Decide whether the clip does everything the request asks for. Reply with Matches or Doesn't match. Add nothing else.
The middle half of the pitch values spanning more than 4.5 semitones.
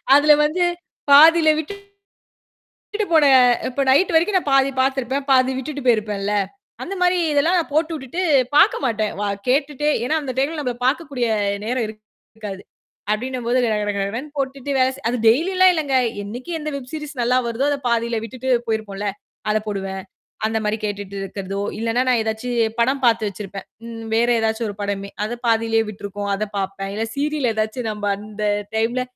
Matches